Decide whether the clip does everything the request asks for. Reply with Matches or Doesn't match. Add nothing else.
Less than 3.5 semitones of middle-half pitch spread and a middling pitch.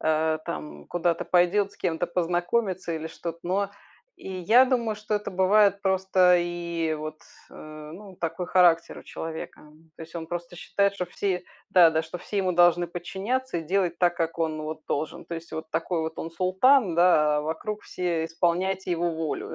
Matches